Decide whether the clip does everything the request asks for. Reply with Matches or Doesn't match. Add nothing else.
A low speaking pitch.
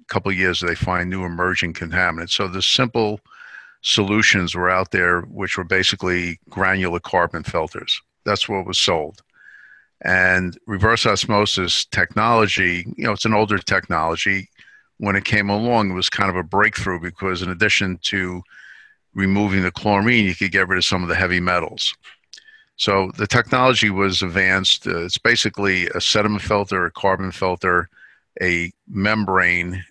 Matches